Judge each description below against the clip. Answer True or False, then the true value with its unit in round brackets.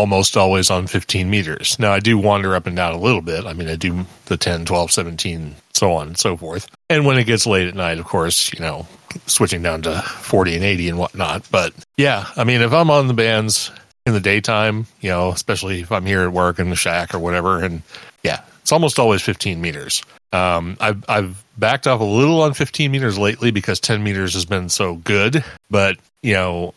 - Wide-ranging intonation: False (3.7 semitones)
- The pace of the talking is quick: True (225 wpm)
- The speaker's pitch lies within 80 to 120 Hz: True (100 Hz)